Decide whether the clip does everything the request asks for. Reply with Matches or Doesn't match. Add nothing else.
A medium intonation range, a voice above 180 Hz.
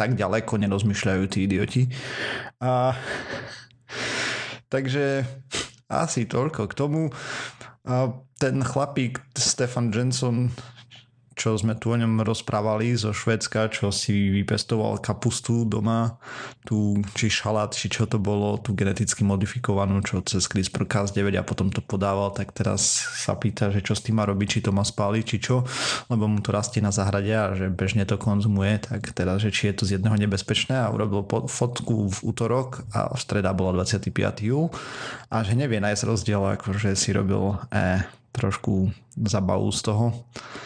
Doesn't match